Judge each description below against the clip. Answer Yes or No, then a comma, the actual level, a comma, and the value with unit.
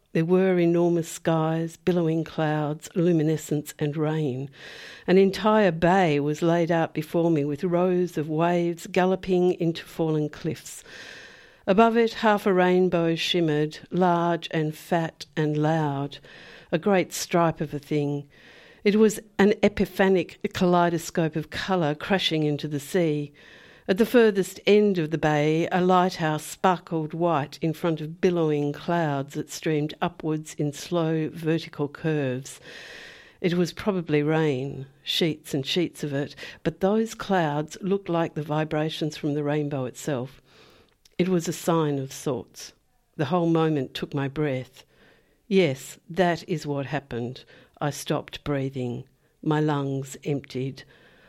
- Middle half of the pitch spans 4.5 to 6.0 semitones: No, average, 3.1 semitones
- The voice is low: No, medium, 160 Hz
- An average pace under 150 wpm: Yes, average, 140 wpm